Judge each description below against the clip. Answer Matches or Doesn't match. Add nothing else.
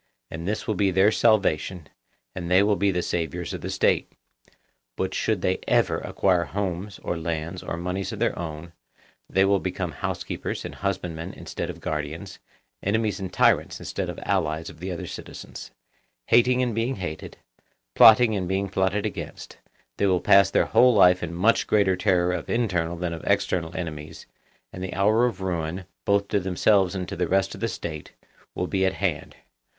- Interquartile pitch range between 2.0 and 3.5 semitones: Matches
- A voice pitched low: Matches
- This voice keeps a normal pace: Matches